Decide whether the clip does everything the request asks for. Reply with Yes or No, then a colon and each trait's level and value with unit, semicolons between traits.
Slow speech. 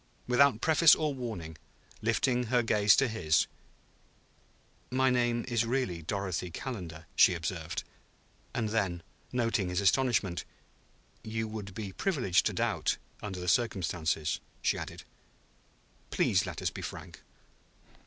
Yes: slow, 125 wpm